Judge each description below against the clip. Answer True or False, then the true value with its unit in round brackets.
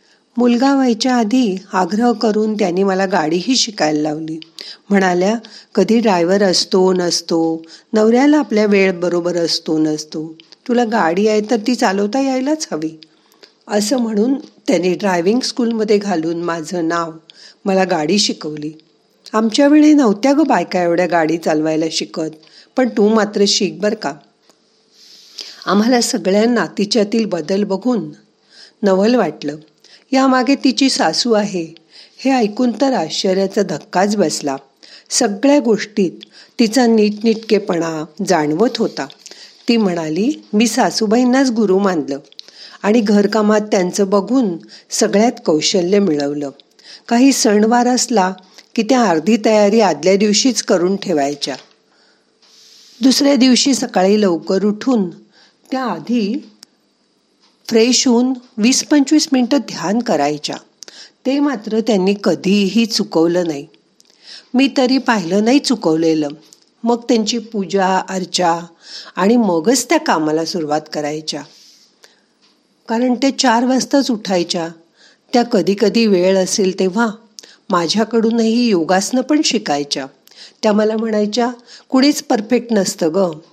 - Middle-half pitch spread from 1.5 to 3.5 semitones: False (5.5 semitones)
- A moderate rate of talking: True (115 wpm)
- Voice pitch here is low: False (210 Hz)